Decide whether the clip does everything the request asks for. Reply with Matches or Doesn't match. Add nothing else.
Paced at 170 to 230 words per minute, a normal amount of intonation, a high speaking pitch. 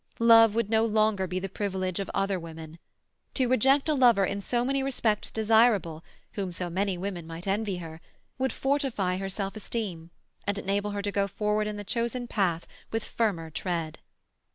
Matches